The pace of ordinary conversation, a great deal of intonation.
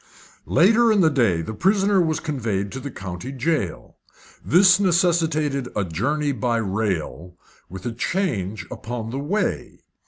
Yes: average, 145 wpm; wide, 8.6 semitones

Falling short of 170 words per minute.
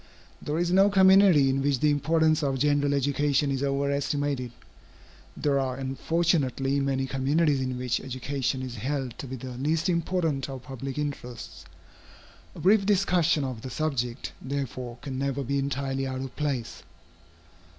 Yes: average, 155 wpm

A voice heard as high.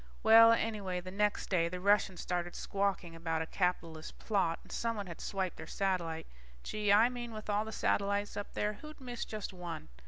Yes: high, 200 Hz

